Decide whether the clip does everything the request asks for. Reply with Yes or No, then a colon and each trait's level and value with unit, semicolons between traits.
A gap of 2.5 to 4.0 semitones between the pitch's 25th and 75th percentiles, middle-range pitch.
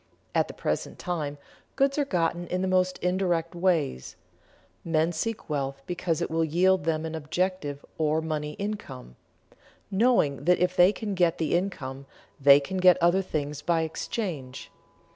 Yes: average, 3.6 semitones; medium, 170 Hz